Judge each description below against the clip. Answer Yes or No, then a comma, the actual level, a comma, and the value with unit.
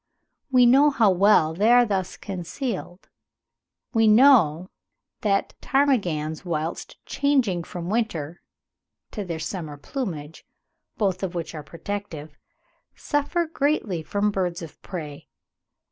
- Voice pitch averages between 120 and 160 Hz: No, high, 190 Hz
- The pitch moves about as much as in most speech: No, wide, 6.2 semitones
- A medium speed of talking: No, slow, 120 wpm